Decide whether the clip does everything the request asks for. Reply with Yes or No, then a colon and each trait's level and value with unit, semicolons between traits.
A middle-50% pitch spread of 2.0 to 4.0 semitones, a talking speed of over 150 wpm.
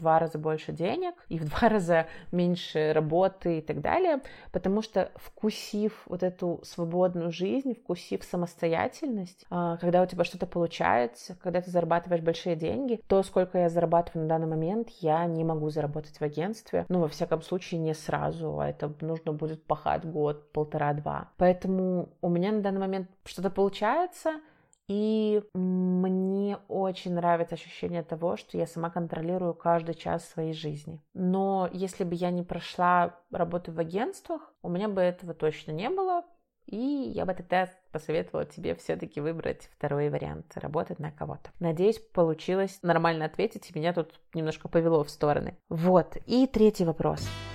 Yes: average, 2.9 semitones; fast, 160 wpm